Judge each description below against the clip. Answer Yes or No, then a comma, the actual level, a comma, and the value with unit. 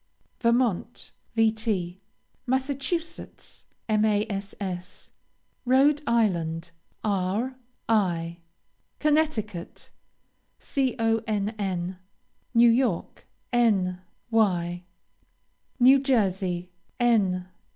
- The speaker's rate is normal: No, slow, 55 wpm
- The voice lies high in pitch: Yes, high, 215 Hz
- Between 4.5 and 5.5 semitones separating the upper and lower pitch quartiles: Yes, average, 4.8 semitones